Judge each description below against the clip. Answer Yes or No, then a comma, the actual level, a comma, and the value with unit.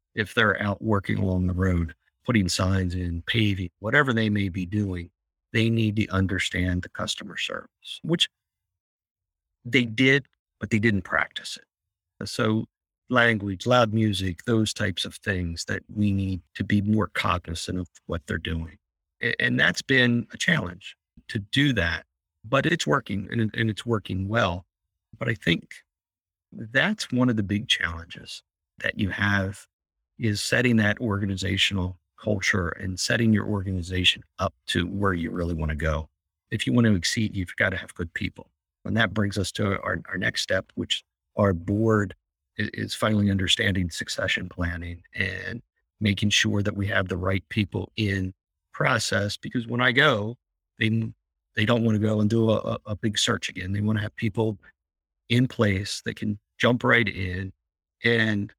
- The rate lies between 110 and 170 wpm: Yes, average, 165 wpm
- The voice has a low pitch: Yes, low, 100 Hz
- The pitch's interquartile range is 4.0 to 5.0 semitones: No, average, 3.6 semitones